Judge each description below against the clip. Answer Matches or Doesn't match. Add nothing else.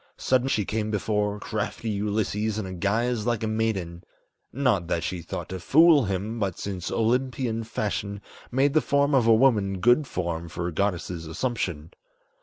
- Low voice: Matches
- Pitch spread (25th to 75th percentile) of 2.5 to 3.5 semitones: Doesn't match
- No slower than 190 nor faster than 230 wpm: Doesn't match